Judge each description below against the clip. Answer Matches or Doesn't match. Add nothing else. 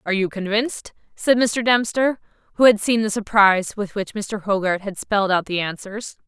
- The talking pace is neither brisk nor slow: Matches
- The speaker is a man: Doesn't match